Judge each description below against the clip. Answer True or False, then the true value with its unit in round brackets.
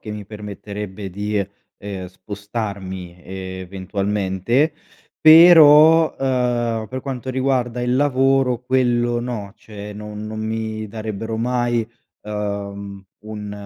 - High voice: False (110 Hz)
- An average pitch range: True (3.6 semitones)